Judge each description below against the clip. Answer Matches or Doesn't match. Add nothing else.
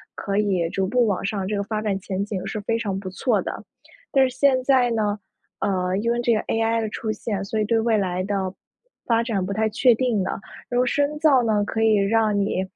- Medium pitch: Doesn't match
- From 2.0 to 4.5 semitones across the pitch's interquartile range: Matches